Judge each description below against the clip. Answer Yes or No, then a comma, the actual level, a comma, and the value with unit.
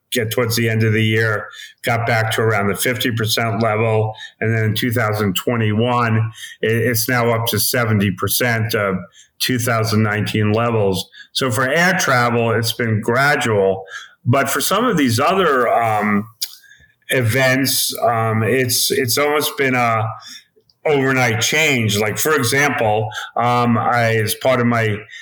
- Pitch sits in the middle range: No, low, 115 Hz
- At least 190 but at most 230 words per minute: No, average, 155 wpm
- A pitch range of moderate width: No, narrow, 2.3 semitones